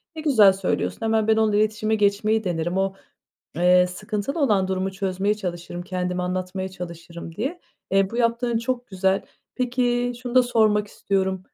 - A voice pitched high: Yes, high, 200 Hz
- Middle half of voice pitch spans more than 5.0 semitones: No, average, 3.5 semitones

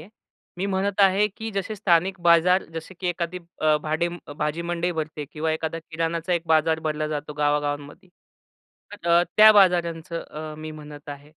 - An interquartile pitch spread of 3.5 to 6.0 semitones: No, average, 2.8 semitones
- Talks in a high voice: No, medium, 165 Hz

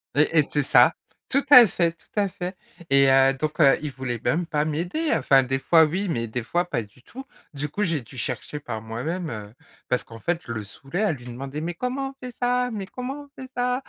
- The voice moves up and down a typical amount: No, wide, 7.0 semitones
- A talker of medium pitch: Yes, medium, 155 Hz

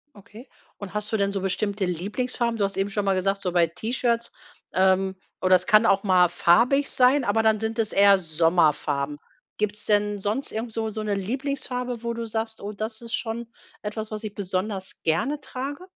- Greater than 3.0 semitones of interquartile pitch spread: Yes, average, 3.4 semitones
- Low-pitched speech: No, high, 210 Hz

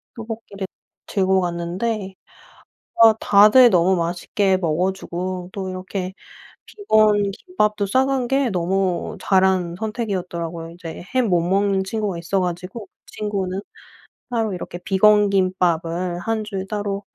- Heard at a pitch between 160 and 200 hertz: Yes, high, 190 Hz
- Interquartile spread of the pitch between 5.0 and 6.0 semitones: No, average, 2.9 semitones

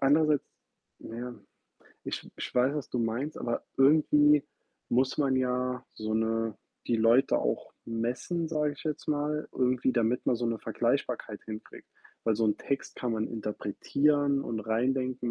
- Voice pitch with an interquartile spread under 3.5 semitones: No, average, 4.0 semitones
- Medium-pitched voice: No, low, 125 Hz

